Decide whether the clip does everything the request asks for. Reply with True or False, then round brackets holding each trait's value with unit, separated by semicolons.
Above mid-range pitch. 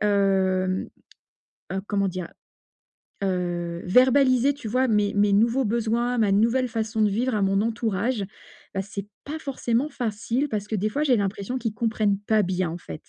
True (215 Hz)